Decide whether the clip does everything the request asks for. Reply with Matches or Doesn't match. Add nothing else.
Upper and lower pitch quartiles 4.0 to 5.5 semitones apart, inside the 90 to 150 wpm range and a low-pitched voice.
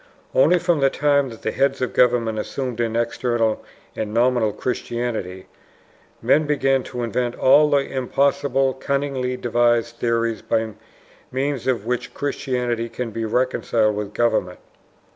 Doesn't match